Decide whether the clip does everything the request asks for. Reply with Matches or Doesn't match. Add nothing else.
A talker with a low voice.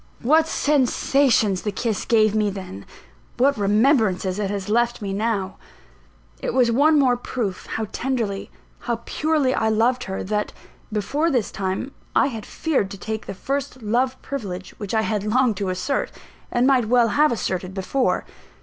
Doesn't match